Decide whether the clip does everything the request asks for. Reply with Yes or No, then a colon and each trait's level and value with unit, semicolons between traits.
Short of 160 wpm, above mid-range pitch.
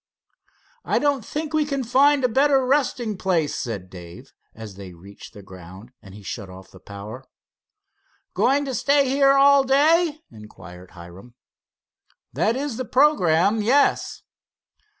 Yes: average, 145 wpm; high, 215 Hz